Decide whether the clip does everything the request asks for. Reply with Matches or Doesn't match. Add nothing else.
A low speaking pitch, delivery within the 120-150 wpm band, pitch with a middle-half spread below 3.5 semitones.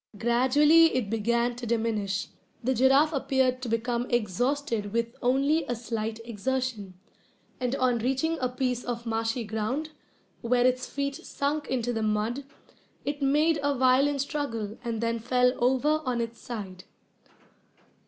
Doesn't match